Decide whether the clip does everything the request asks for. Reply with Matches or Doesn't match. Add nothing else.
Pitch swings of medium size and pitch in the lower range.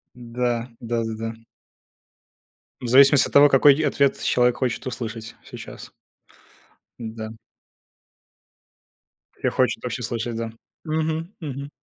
Matches